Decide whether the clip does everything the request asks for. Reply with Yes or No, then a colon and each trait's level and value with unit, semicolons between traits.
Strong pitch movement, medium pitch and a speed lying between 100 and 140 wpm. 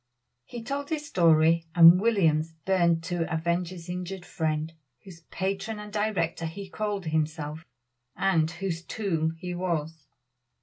No: average, 3.1 semitones; medium, 175 Hz; slow, 135 wpm